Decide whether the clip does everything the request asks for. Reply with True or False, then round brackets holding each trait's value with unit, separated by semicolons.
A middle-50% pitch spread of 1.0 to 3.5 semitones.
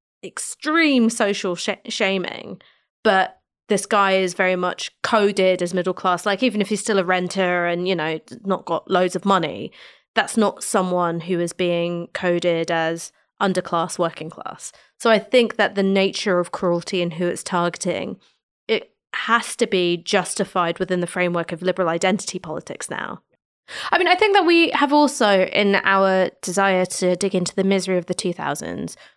True (2.5 semitones)